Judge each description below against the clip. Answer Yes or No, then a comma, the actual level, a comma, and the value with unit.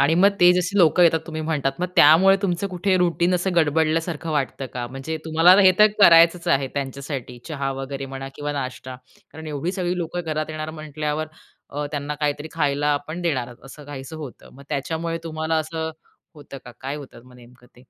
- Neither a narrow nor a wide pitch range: Yes, average, 3.3 semitones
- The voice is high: No, medium, 155 Hz